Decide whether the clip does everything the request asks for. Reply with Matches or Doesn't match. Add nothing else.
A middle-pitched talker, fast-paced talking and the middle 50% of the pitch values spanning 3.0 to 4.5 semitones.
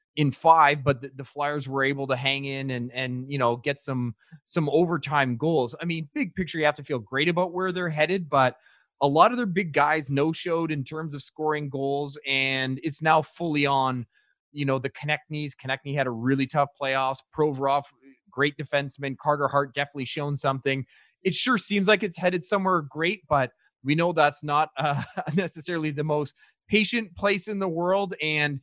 Doesn't match